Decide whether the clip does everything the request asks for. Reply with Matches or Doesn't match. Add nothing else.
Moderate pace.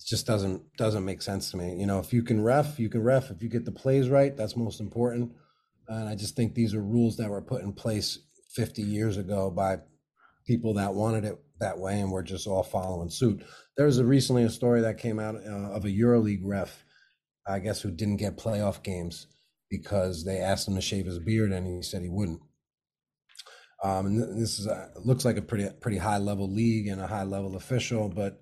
Doesn't match